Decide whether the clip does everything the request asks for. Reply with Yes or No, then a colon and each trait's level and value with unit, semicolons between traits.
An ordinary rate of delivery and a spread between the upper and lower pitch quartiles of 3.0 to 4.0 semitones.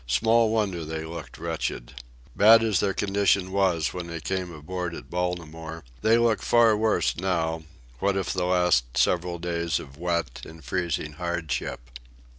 Yes: average, 155 wpm; average, 3.3 semitones